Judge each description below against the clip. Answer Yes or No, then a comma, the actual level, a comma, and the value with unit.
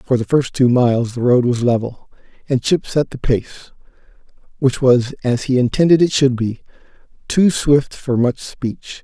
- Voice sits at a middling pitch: No, low, 130 Hz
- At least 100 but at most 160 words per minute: No, average, 175 wpm